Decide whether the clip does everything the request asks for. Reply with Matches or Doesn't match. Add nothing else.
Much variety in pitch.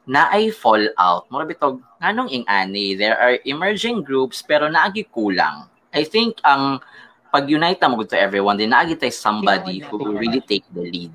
Matches